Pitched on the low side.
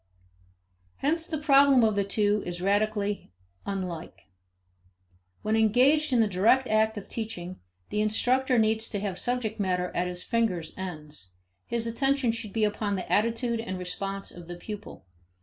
No: high, 215 Hz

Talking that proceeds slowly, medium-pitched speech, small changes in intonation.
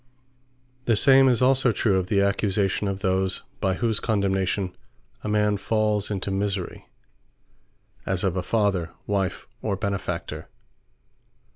No: slow, 130 wpm; low, 100 Hz; narrow, 1.9 semitones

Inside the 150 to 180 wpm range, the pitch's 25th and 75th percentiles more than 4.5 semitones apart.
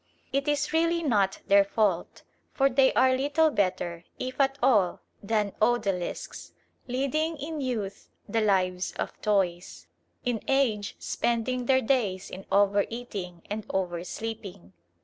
No: slow, 135 wpm; wide, 5.6 semitones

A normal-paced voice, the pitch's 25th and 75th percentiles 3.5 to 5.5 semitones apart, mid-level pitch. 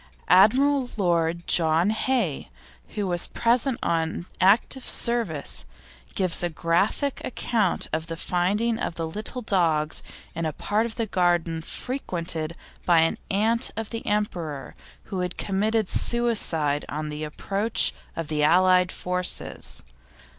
No: slow, 130 wpm; average, 5.1 semitones; medium, 180 Hz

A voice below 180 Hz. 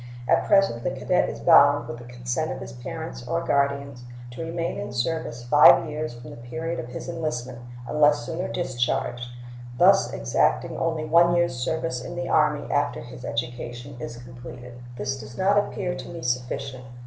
Yes: low, 135 Hz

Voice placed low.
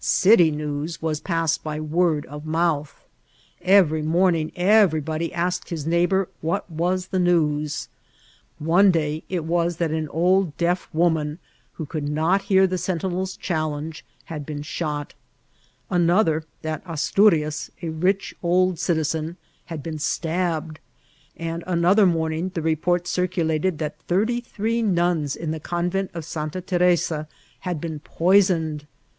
No: medium, 165 Hz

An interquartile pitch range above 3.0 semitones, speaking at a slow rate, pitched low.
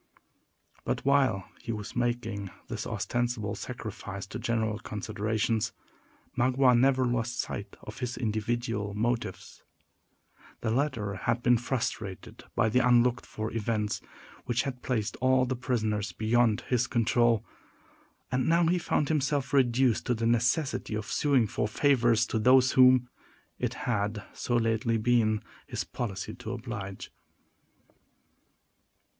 No: average, 2.7 semitones; slow, 130 wpm; low, 120 Hz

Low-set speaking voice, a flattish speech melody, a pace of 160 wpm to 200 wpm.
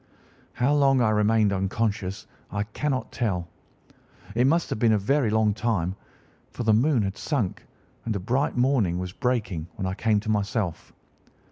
No: low, 110 Hz; average, 3.8 semitones; average, 165 wpm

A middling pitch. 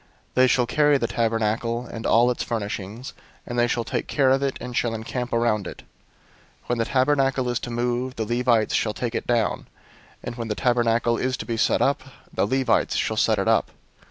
No: low, 120 Hz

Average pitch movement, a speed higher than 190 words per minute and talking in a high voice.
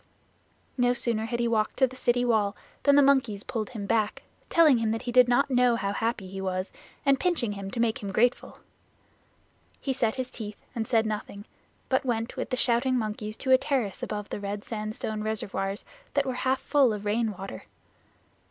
Yes: average, 3.3 semitones; average, 200 wpm; high, 230 Hz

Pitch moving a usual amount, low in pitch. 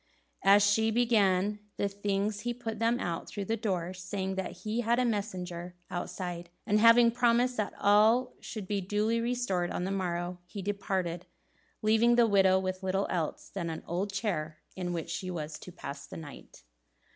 No: average, 3.5 semitones; high, 195 Hz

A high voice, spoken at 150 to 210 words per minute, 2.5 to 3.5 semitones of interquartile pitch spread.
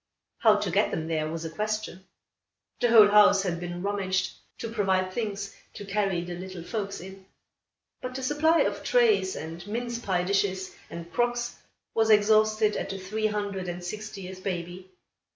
Yes: high, 200 Hz; average, 170 wpm; average, 2.9 semitones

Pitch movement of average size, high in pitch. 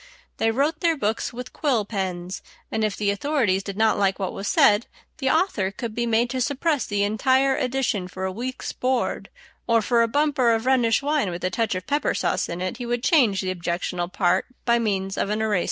Yes: average, 5.0 semitones; high, 225 Hz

